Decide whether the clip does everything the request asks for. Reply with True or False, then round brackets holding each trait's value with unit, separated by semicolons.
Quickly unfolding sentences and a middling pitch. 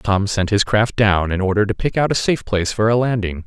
False (275 wpm; 105 Hz)